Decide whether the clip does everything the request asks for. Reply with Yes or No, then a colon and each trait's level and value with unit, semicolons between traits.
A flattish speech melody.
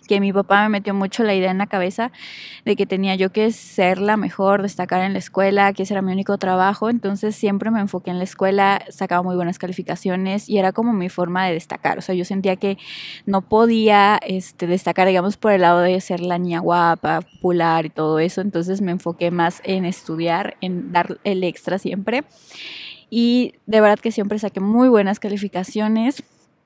Yes: narrow, 2.3 semitones